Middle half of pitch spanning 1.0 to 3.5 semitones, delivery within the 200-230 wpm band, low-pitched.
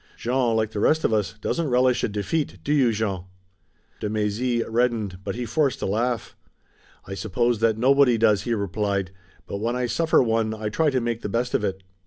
Yes: average, 3.1 semitones; fast, 205 wpm; low, 115 Hz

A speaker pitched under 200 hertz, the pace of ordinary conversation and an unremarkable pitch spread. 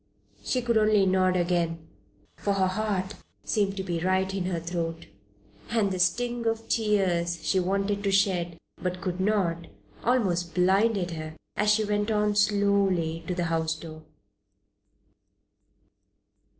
Yes: high, 190 Hz; average, 145 wpm; average, 3.2 semitones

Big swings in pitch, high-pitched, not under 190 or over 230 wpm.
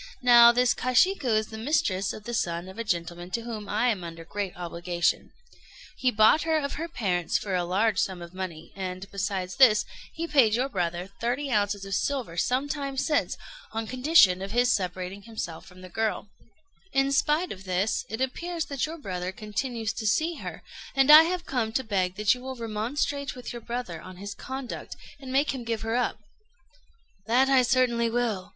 Yes: wide, 5.7 semitones; high, 225 Hz; average, 195 wpm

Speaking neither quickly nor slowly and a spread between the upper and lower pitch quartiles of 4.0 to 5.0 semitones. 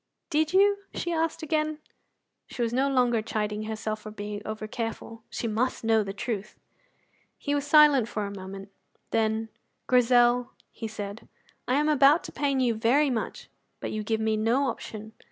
Yes: average, 170 wpm; average, 4.4 semitones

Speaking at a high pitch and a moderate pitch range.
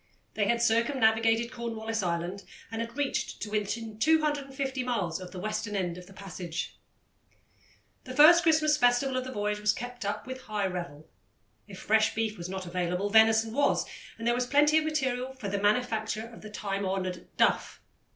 Yes: high, 220 Hz; average, 4.3 semitones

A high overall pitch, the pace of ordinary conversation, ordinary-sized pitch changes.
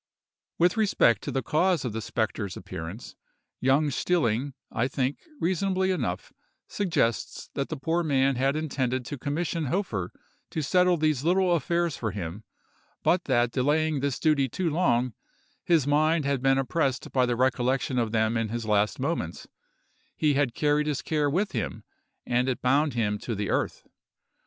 No: low, 135 Hz; average, 160 wpm; average, 4.8 semitones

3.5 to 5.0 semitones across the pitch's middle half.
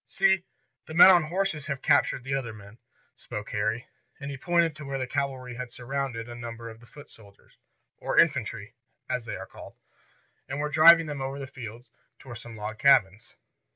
Yes: average, 4.0 semitones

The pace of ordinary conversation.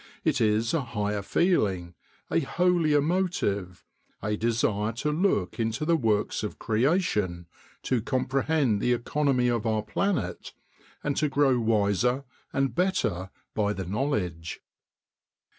No: slow, 125 wpm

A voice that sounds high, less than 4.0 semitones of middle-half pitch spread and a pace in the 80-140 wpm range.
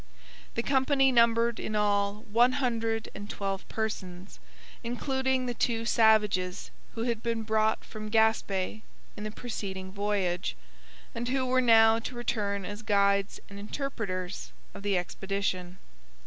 Yes: high, 220 Hz; average, 2.8 semitones; slow, 135 wpm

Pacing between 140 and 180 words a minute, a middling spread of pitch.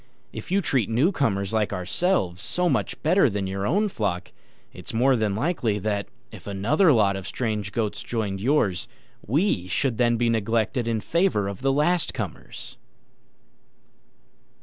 No: average, 150 wpm; wide, 6.0 semitones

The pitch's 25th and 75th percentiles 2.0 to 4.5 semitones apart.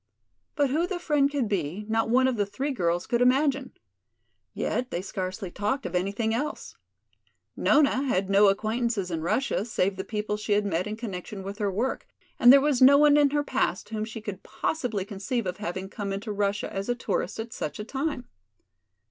No: average, 5.0 semitones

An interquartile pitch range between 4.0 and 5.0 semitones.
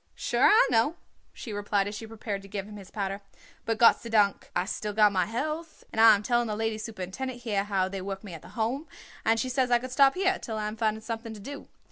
No: average, 2.9 semitones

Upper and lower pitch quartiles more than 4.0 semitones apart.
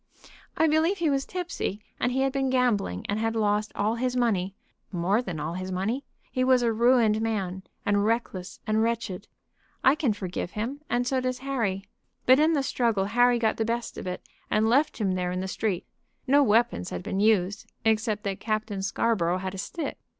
Yes: average, 4.5 semitones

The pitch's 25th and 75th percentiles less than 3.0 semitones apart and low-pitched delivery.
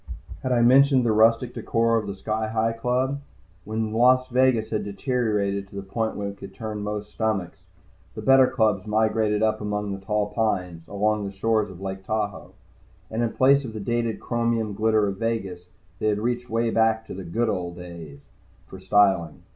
Yes: narrow, 2.6 semitones; low, 110 Hz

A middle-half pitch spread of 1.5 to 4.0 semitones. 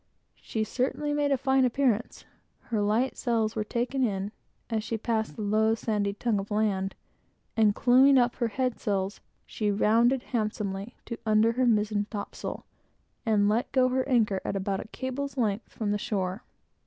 Yes: average, 3.2 semitones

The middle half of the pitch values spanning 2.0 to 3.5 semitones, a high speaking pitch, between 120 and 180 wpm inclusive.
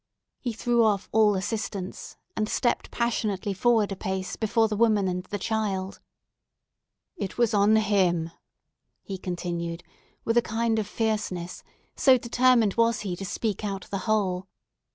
Yes: average, 3.0 semitones; high, 210 Hz; average, 150 wpm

